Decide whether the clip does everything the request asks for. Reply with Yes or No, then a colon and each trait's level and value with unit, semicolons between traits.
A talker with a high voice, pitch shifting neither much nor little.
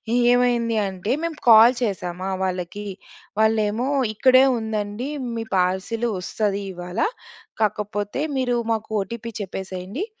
Yes: high, 215 Hz; average, 3.7 semitones